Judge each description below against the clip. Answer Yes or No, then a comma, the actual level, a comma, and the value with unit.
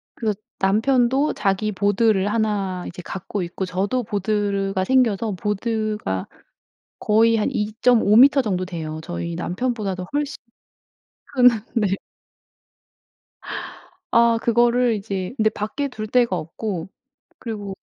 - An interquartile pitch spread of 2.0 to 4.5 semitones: Yes, average, 3.4 semitones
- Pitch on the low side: No, high, 210 Hz